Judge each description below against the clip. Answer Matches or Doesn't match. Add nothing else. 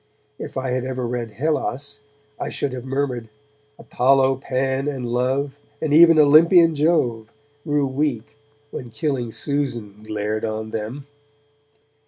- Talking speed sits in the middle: Doesn't match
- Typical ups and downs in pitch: Matches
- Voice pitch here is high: Doesn't match